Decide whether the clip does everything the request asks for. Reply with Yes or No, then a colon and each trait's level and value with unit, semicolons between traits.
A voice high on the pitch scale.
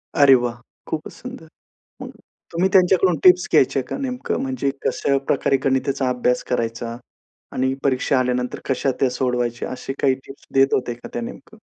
No: low, 130 Hz